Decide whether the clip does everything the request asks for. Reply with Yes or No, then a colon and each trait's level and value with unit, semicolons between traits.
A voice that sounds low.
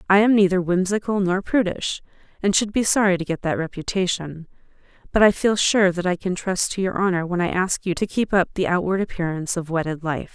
No: medium, 185 Hz